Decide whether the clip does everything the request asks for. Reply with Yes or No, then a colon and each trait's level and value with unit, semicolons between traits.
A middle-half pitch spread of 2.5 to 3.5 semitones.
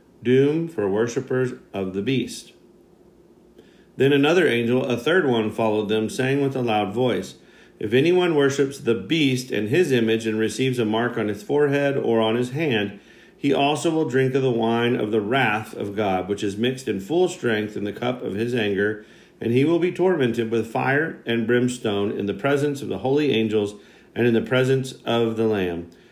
No: average, 4.0 semitones